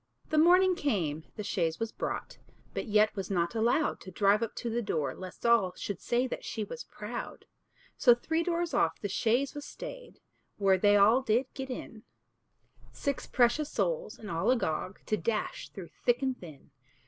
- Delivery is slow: No, average, 185 wpm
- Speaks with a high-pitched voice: Yes, high, 225 Hz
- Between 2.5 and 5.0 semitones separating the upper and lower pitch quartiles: No, wide, 5.5 semitones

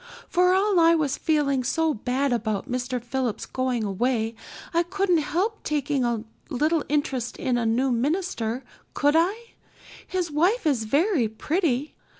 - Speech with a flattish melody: No, wide, 5.5 semitones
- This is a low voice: No, very high, 280 Hz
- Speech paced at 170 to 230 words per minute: No, average, 150 wpm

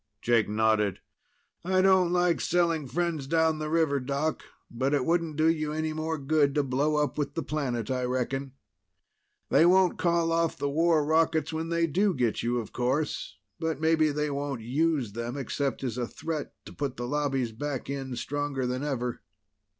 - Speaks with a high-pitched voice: No, medium, 145 Hz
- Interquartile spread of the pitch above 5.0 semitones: No, average, 3.9 semitones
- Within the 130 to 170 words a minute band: No, average, 180 wpm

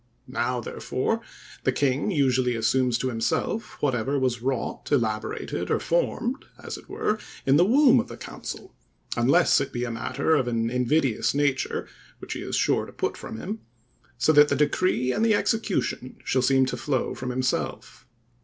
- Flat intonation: No, average, 3.3 semitones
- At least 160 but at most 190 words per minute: Yes, average, 170 wpm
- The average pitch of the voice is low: Yes, low, 130 Hz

